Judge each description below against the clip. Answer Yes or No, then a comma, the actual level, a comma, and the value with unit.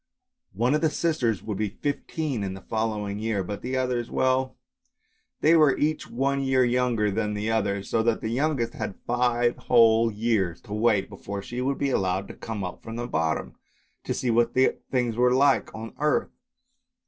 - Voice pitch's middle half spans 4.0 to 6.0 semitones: No, average, 3.6 semitones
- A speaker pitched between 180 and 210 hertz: No, low, 115 Hz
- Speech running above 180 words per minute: Yes, average, 190 wpm